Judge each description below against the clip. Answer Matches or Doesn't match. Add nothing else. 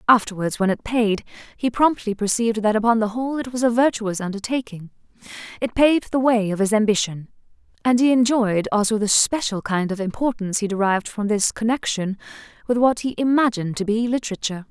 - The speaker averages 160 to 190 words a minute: Matches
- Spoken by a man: Doesn't match